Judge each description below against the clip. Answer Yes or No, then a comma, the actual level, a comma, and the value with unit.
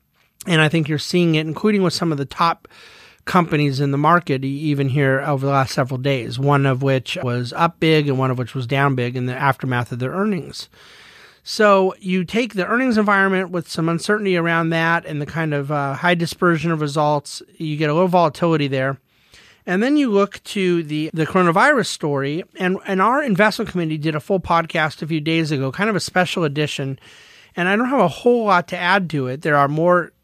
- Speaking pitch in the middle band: Yes, medium, 165 Hz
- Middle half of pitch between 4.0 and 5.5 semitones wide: Yes, average, 4.6 semitones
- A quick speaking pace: Yes, fast, 215 wpm